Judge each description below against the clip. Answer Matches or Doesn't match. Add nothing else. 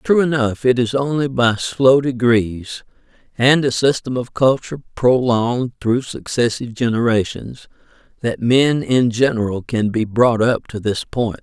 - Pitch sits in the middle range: Doesn't match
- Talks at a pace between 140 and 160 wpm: Matches